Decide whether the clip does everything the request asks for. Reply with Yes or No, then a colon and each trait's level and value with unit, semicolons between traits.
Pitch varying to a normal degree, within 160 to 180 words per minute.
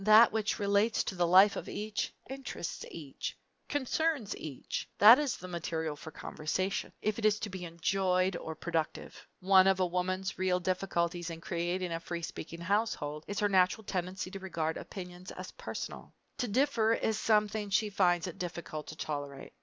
Yes: average, 3.5 semitones; average, 175 wpm